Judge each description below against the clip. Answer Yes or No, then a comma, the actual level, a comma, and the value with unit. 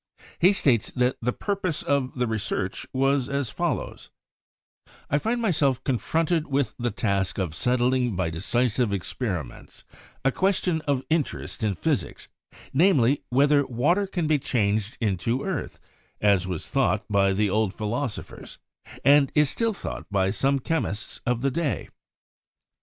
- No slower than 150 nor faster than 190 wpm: No, average, 140 wpm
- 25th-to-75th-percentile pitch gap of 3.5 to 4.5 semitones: No, wide, 5.6 semitones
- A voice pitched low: Yes, low, 125 Hz